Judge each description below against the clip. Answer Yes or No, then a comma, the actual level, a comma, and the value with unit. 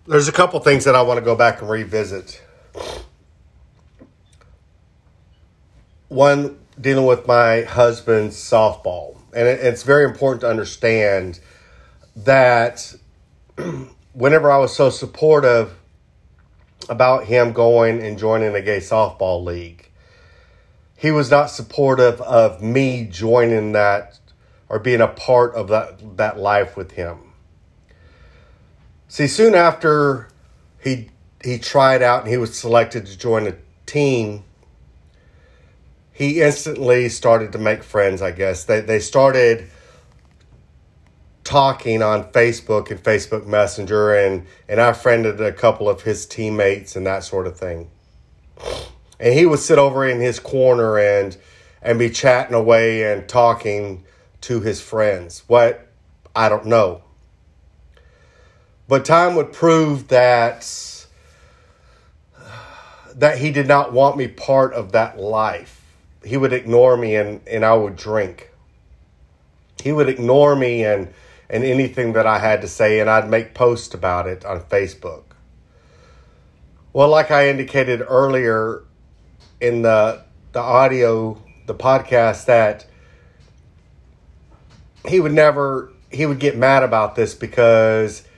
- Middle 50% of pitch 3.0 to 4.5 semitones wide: No, average, 4.9 semitones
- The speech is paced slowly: Yes, slow, 130 wpm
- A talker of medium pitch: No, low, 110 Hz